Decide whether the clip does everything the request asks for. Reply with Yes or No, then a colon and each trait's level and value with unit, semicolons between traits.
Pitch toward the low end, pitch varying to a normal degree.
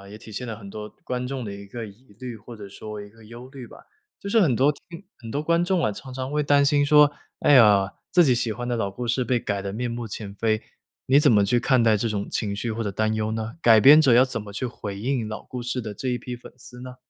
Yes: low, 120 Hz; average, 3.4 semitones